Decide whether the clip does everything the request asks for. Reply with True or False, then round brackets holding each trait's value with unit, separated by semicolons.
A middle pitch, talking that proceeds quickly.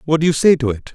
True (145 Hz; 380 wpm)